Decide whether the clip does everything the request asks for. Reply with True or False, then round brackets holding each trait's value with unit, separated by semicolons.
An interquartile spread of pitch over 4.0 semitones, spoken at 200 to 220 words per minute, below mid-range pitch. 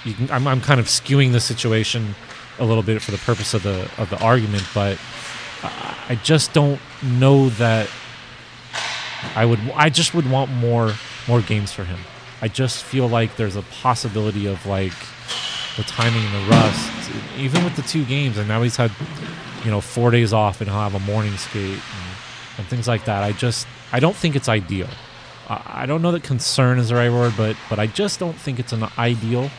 False (3.4 semitones; 205 wpm; 120 Hz)